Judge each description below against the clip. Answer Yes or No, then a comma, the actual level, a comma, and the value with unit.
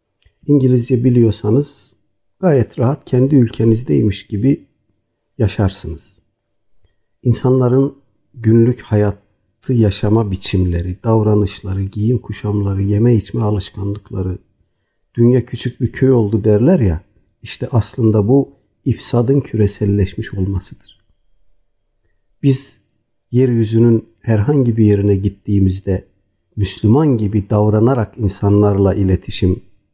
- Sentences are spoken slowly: Yes, slow, 85 wpm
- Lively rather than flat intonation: No, average, 3.4 semitones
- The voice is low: Yes, low, 105 Hz